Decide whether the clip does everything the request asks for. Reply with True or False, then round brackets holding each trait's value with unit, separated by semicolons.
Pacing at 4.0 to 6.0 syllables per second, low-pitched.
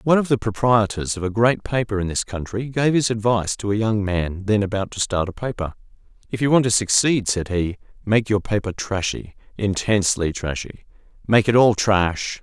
True (5.4 syllables/s; 105 Hz)